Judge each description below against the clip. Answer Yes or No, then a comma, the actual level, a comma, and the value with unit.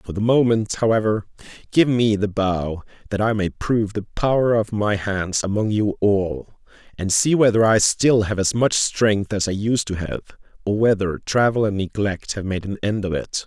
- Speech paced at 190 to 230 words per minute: Yes, average, 200 wpm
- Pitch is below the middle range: Yes, low, 105 Hz